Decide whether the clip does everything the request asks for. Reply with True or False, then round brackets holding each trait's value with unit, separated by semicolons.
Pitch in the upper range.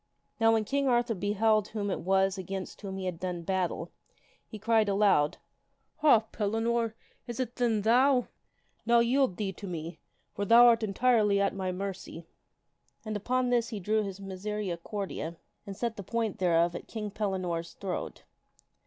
True (205 Hz)